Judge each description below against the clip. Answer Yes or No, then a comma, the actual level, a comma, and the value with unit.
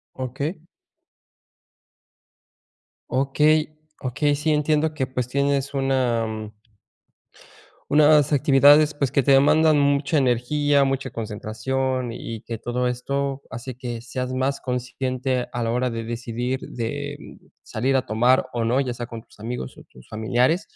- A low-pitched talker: Yes, low, 130 Hz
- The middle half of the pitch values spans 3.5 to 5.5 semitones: No, average, 2.8 semitones